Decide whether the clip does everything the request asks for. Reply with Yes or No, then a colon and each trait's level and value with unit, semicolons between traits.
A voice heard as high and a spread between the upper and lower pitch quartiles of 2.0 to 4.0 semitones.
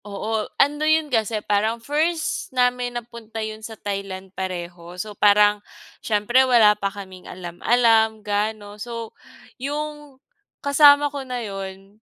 Yes: high, 220 Hz; average, 3.6 semitones